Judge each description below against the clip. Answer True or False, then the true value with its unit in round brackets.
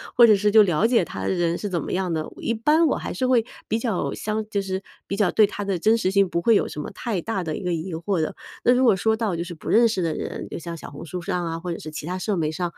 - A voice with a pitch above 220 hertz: False (190 Hz)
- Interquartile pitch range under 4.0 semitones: False (4.4 semitones)